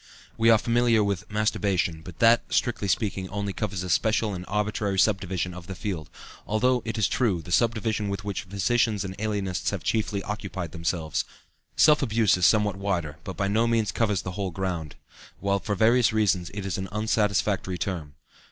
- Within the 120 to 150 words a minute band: No, average, 180 wpm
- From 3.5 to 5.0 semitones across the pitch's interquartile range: No, average, 2.8 semitones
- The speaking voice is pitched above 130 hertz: No, low, 100 Hz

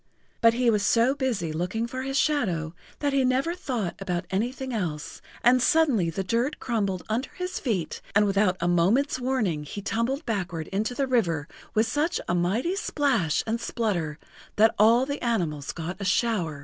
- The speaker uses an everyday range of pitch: No, wide, 6.3 semitones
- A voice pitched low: No, high, 225 Hz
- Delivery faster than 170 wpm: Yes, average, 180 wpm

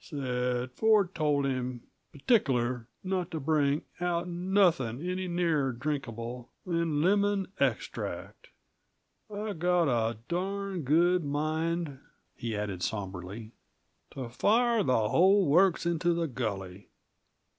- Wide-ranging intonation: Yes, wide, 6.4 semitones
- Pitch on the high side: No, medium, 155 Hz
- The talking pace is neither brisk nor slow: No, slow, 115 wpm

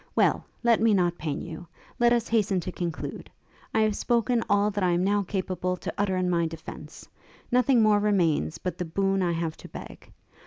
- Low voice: No, high, 190 Hz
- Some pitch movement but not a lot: Yes, average, 3.7 semitones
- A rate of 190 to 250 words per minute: Yes, average, 200 wpm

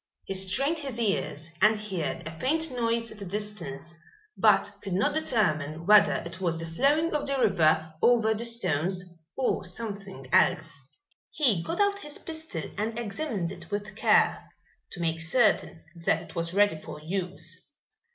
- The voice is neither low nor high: No, high, 200 Hz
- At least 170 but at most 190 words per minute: No, average, 160 wpm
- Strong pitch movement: Yes, wide, 5.9 semitones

